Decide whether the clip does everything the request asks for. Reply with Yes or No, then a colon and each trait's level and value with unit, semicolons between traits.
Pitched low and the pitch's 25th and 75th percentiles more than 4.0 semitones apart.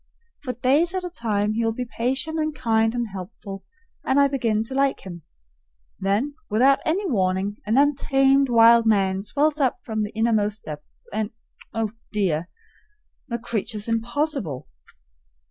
No: high, 230 Hz; average, 4.7 semitones